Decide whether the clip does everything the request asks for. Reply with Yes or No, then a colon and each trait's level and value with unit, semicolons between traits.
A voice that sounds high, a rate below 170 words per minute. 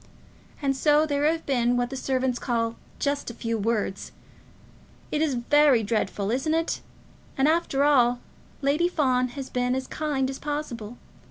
Yes: very high, 265 Hz; average, 160 wpm